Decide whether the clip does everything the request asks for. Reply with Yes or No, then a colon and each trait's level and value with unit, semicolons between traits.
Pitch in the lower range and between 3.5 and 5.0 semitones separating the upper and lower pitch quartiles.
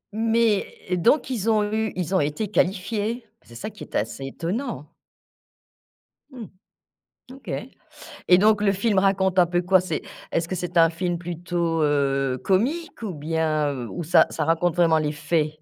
No: medium, 175 Hz; average, 4.7 semitones